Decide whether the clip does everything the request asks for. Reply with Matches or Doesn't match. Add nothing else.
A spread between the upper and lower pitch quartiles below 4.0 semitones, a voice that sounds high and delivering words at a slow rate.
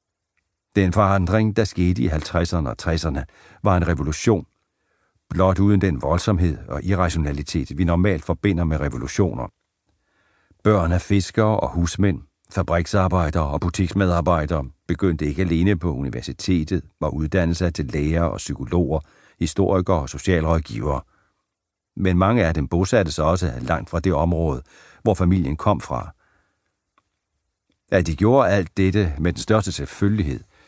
Doesn't match